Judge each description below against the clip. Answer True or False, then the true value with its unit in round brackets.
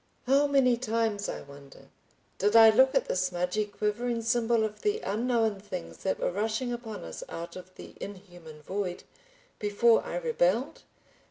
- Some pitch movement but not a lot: True (4.3 semitones)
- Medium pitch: False (215 Hz)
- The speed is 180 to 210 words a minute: False (160 wpm)